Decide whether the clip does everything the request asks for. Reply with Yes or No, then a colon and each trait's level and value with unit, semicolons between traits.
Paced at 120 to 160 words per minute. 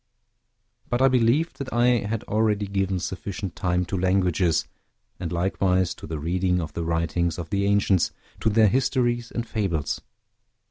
Yes: average, 155 wpm